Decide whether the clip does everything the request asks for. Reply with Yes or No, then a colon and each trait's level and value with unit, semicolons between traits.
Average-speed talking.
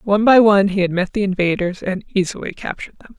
No: fast, 225 wpm